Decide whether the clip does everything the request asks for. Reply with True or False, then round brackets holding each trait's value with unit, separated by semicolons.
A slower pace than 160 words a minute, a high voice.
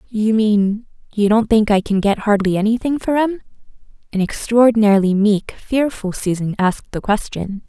True (150 wpm; 215 Hz)